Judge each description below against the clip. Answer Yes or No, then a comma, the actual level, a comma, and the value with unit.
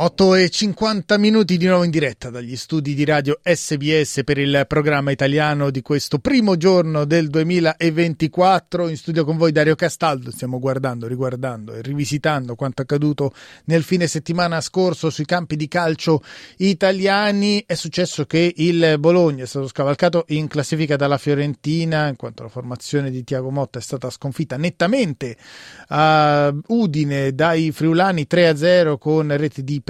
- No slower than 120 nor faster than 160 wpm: Yes, average, 155 wpm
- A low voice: No, medium, 155 Hz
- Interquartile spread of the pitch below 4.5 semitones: Yes, average, 3.4 semitones